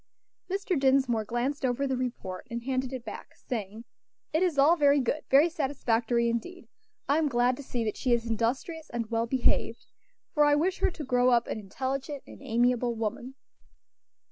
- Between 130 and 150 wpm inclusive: No, average, 180 wpm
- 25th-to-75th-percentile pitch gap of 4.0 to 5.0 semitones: No, average, 3.4 semitones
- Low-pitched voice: No, very high, 255 Hz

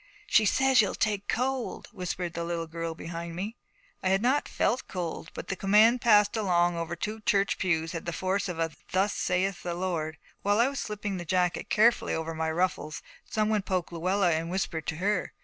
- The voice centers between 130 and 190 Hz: Yes, medium, 185 Hz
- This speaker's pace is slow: No, average, 200 wpm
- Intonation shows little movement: No, average, 3.7 semitones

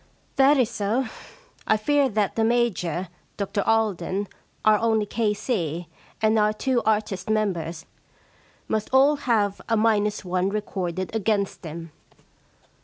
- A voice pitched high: Yes, high, 210 Hz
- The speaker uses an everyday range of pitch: Yes, average, 3.0 semitones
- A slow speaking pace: Yes, slow, 130 wpm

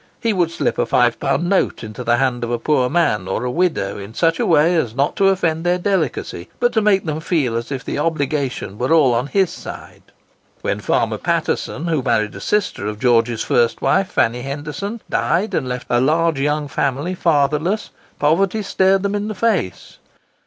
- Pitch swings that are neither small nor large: No, wide, 6.7 semitones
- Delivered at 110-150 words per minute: No, average, 200 wpm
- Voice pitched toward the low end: No, medium, 150 Hz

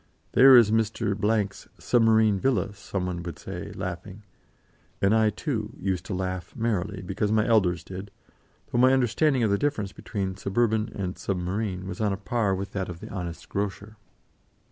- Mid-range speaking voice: No, low, 100 Hz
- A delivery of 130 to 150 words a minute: No, average, 170 wpm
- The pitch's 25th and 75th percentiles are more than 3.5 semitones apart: No, average, 2.9 semitones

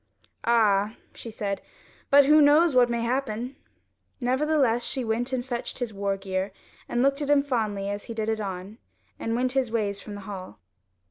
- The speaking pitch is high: Yes, high, 230 Hz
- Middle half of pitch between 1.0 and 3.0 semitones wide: No, average, 4.2 semitones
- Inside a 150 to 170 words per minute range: No, average, 185 wpm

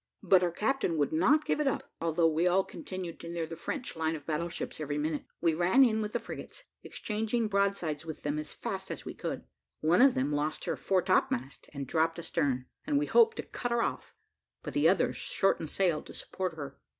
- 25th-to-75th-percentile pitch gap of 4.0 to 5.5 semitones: Yes, average, 5.2 semitones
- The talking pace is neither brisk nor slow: No, fast, 220 wpm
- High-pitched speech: No, medium, 170 Hz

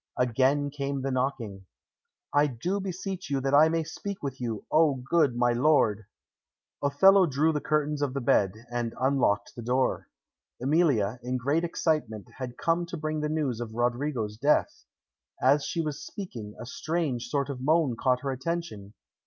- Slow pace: No, average, 170 wpm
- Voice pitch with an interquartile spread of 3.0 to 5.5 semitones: Yes, average, 4.2 semitones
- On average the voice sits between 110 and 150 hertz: Yes, medium, 140 Hz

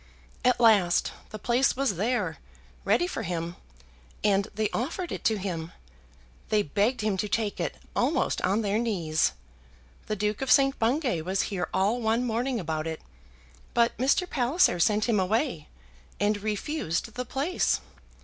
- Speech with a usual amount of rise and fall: Yes, average, 4.5 semitones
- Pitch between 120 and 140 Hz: No, high, 215 Hz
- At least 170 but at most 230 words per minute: No, average, 155 wpm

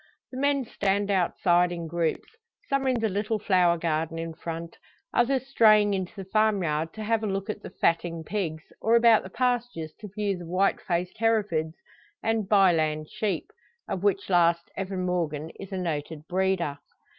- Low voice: No, high, 190 Hz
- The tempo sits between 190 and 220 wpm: No, average, 175 wpm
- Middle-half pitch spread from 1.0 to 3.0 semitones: No, average, 4.3 semitones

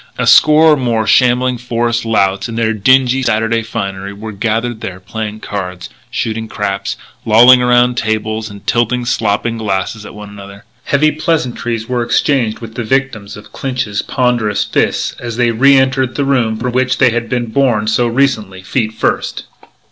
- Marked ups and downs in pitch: No, narrow, 2.6 semitones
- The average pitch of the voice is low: Yes, low, 115 Hz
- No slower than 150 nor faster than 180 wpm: Yes, average, 170 wpm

